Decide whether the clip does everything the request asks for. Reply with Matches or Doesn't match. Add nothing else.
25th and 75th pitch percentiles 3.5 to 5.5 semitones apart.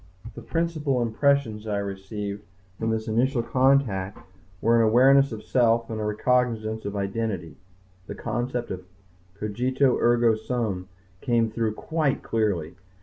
Doesn't match